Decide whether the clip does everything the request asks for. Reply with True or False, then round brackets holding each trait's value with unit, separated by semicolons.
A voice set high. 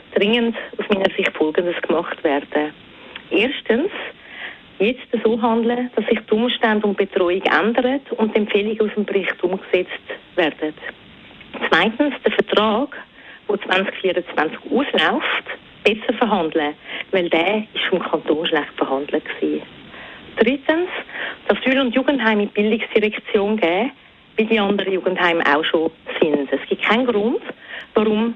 True (210 Hz)